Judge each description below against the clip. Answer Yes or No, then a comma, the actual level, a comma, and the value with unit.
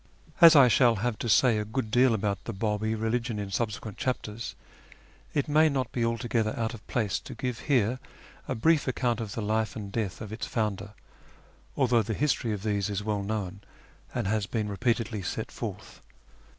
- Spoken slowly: No, average, 190 wpm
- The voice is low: Yes, low, 110 Hz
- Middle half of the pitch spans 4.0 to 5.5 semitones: No, average, 2.7 semitones